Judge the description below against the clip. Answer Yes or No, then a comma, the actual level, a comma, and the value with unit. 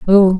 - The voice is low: No, high, 190 Hz